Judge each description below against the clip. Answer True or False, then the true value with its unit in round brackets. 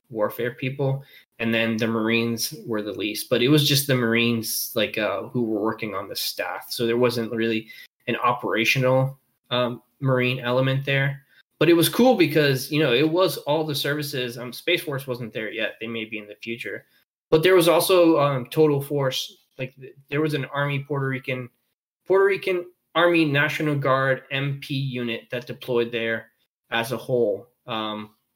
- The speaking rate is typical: True (180 wpm)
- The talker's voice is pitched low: True (130 Hz)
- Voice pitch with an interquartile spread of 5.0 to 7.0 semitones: False (3.8 semitones)